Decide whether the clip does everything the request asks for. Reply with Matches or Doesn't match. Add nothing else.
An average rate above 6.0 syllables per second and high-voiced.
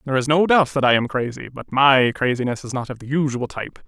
Doesn't match